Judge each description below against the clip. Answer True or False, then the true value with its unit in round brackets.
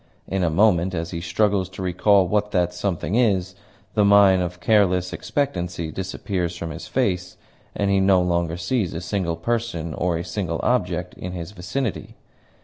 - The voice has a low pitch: True (90 Hz)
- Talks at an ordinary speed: True (170 wpm)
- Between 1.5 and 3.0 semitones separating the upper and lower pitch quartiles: True (2.7 semitones)